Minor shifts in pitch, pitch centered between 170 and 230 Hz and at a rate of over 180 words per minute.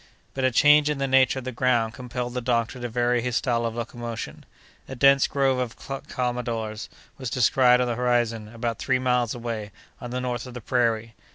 No: narrow, 1.6 semitones; low, 125 Hz; average, 200 wpm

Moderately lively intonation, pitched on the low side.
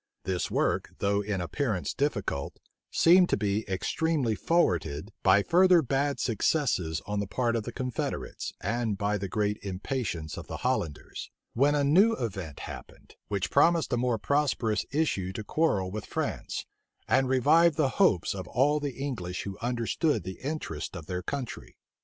No: wide, 6.8 semitones; low, 115 Hz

